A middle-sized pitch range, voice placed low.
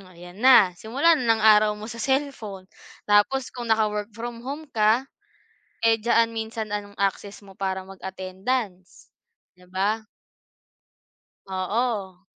No: average, 3.2 semitones; high, 215 Hz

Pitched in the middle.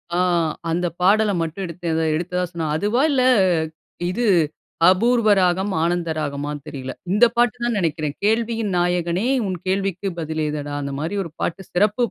Yes: medium, 180 Hz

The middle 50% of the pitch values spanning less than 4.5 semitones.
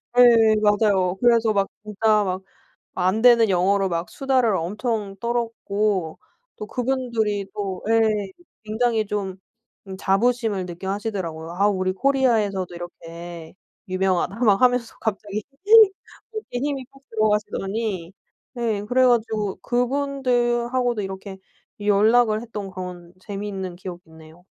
Yes: average, 3.8 semitones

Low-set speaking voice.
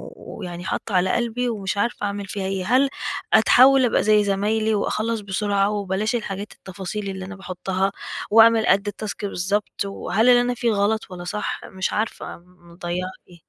No: high, 200 Hz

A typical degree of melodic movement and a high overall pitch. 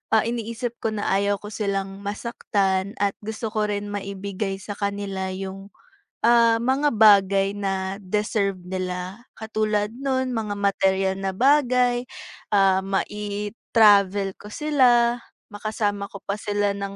No: narrow, 2.3 semitones; high, 205 Hz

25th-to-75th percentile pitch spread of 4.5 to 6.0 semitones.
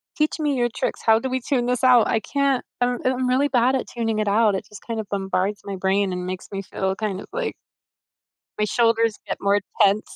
No: average, 4.1 semitones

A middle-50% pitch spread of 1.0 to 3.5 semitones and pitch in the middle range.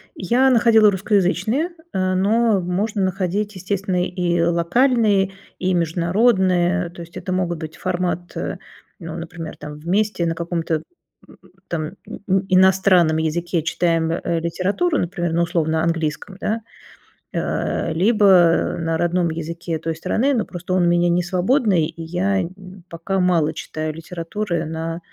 Yes: average, 2.7 semitones; medium, 175 Hz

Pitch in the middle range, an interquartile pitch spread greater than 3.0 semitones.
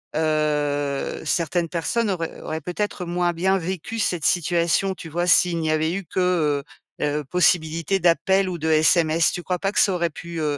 No: medium, 170 Hz; narrow, 2.4 semitones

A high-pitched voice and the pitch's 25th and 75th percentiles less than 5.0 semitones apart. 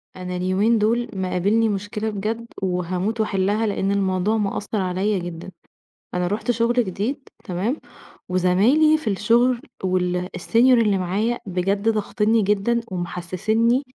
Yes: high, 205 Hz; average, 3.6 semitones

